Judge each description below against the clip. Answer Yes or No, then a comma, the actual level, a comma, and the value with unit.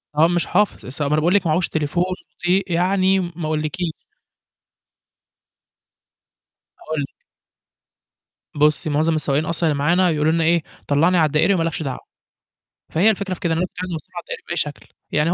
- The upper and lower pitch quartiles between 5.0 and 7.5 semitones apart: No, average, 2.8 semitones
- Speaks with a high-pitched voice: No, medium, 165 Hz